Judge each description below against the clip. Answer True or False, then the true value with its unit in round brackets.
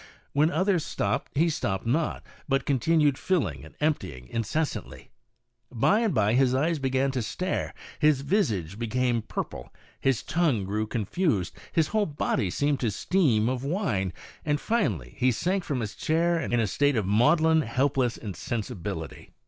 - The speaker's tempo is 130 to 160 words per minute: True (155 wpm)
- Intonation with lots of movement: True (6.8 semitones)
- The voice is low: True (130 Hz)